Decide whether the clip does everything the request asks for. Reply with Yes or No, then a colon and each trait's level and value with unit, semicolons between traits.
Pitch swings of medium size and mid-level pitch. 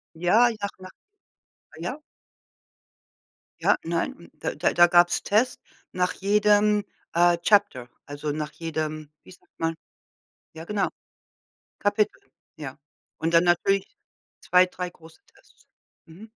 Yes: average, 3.8 semitones; medium, 175 Hz